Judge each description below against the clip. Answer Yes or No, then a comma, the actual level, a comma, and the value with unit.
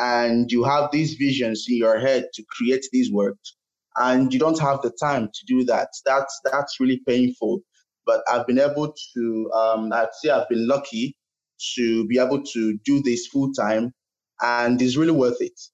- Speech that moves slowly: No, average, 185 wpm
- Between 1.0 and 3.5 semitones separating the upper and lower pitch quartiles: Yes, average, 2.9 semitones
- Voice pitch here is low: Yes, low, 125 Hz